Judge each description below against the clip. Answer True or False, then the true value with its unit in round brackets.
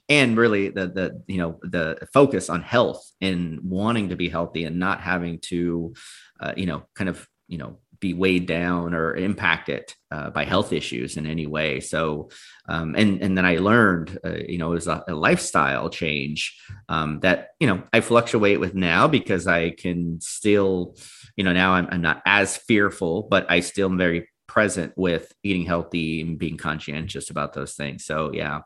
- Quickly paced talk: False (190 wpm)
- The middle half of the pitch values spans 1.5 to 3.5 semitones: True (2.9 semitones)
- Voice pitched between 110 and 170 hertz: False (85 Hz)